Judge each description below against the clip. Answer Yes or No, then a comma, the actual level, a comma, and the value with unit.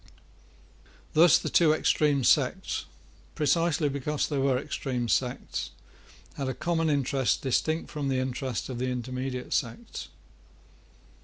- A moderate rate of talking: No, slow, 125 wpm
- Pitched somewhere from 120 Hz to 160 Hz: Yes, low, 135 Hz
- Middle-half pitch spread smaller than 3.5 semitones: Yes, average, 3.0 semitones